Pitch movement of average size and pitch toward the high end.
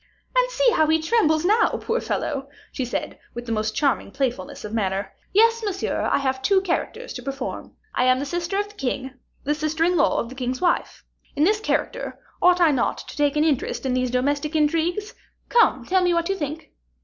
No: wide, 5.9 semitones; very high, 305 Hz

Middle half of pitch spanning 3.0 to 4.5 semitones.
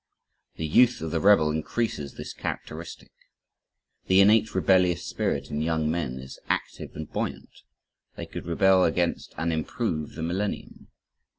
Yes: average, 3.6 semitones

